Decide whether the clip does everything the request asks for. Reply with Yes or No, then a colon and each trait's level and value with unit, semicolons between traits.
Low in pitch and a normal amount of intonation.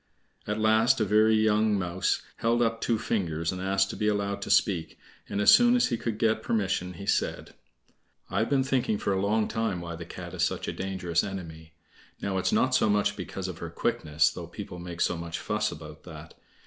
Yes: low, 100 Hz; average, 3.7 semitones